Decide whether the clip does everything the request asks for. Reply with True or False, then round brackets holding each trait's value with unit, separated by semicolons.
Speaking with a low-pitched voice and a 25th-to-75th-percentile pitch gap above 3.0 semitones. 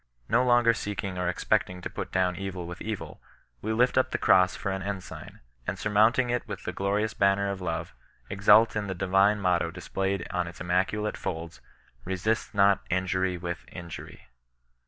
False (95 Hz; 2.6 semitones)